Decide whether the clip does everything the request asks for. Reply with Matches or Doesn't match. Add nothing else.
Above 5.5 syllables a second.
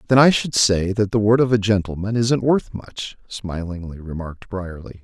Doesn't match